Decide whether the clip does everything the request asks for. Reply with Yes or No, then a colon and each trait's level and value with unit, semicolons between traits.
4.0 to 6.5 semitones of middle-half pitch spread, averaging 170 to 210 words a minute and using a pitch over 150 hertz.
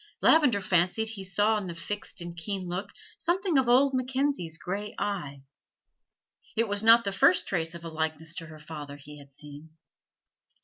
Yes: wide, 5.6 semitones; average, 175 wpm; medium, 185 Hz